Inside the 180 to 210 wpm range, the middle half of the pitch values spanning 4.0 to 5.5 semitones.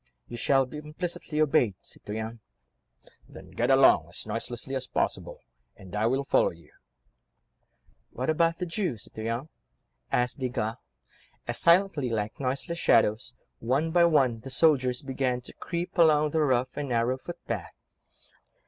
No: average, 140 wpm; average, 4.8 semitones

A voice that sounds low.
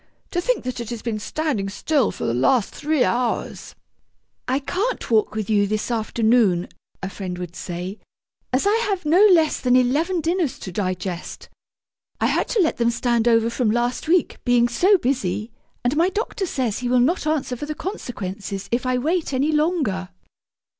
No: high, 245 Hz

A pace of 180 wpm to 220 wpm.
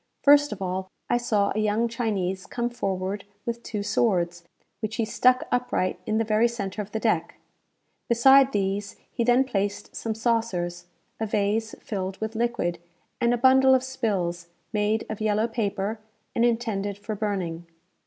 No: average, 165 wpm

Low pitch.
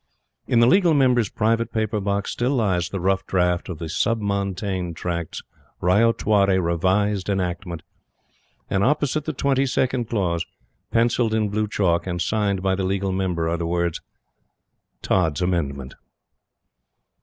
Yes: very low, 95 Hz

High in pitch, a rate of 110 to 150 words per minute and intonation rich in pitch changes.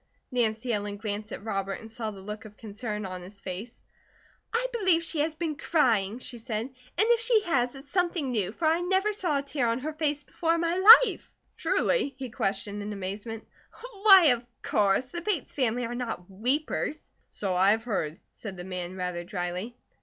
No: high, 235 Hz; average, 195 wpm; wide, 7.4 semitones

